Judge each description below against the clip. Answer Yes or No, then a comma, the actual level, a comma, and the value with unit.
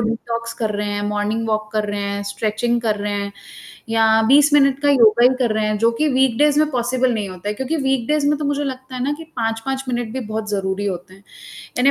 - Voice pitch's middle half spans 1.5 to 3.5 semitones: No, average, 4.1 semitones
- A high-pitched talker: Yes, high, 230 Hz